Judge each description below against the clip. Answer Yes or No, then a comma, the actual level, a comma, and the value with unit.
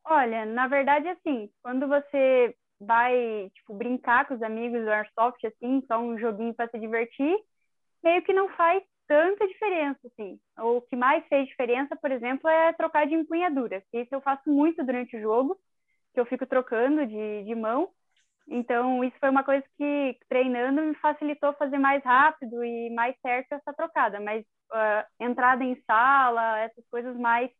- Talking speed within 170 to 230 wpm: Yes, average, 175 wpm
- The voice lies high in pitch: Yes, very high, 255 Hz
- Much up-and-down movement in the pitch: No, average, 3.9 semitones